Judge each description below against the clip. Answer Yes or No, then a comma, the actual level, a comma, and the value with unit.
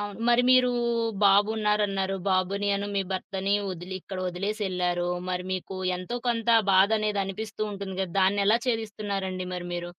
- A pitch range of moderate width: No, narrow, 2.2 semitones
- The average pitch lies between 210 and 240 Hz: No, high, 195 Hz